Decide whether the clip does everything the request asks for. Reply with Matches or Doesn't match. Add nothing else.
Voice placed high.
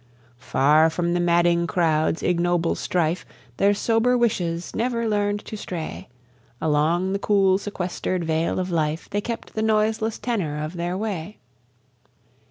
Doesn't match